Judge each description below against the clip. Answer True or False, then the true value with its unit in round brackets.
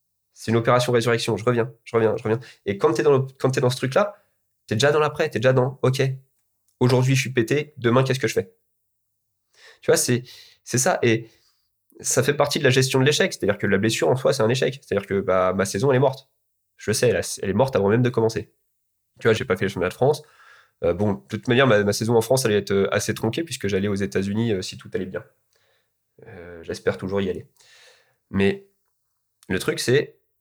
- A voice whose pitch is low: True (115 Hz)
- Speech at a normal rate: False (235 wpm)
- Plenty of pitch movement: False (4.1 semitones)